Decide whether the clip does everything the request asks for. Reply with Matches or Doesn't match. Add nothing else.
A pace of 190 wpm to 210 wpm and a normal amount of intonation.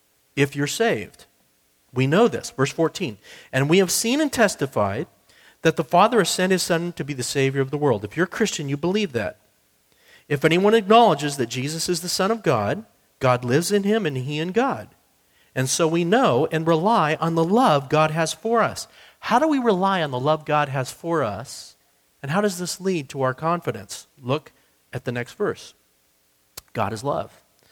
Doesn't match